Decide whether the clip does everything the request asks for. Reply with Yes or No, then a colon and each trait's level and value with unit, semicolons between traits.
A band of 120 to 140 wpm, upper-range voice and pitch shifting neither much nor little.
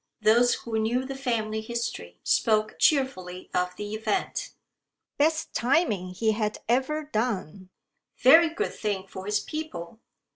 Yes: slow, 135 wpm; high, 220 Hz; average, 4.4 semitones